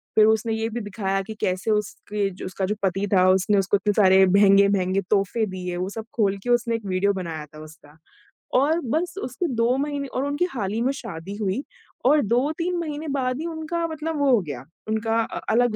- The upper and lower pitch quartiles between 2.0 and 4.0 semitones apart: No, average, 5.1 semitones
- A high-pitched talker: Yes, high, 215 Hz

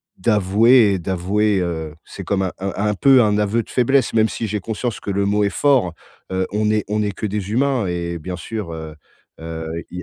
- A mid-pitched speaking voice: No, low, 105 Hz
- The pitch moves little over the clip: No, average, 3.1 semitones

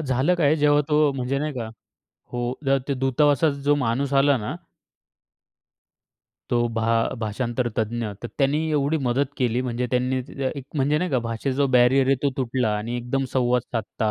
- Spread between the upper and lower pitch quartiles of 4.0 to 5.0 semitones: No, average, 2.8 semitones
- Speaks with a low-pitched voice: Yes, low, 130 Hz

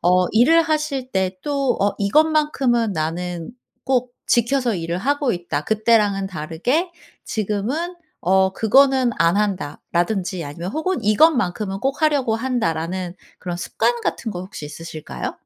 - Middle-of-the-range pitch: No, high, 215 Hz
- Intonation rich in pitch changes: Yes, wide, 6.8 semitones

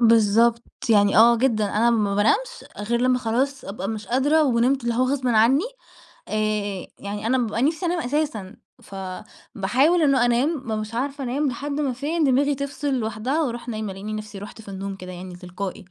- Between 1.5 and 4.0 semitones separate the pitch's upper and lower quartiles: No, average, 4.6 semitones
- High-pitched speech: Yes, high, 235 Hz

